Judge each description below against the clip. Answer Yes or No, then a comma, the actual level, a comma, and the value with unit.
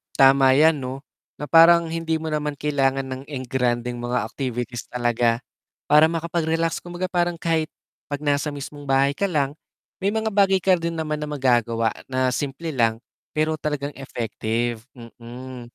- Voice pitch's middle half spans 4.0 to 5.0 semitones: Yes, average, 4.4 semitones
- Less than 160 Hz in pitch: Yes, medium, 140 Hz